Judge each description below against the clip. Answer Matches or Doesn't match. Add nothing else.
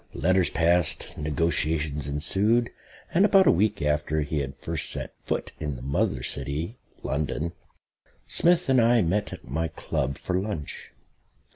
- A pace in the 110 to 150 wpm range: Matches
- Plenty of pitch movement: Matches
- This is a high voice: Doesn't match